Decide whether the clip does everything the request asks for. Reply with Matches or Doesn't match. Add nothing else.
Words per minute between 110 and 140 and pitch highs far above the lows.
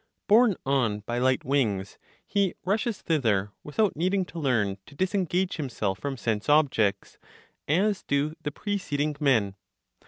Matches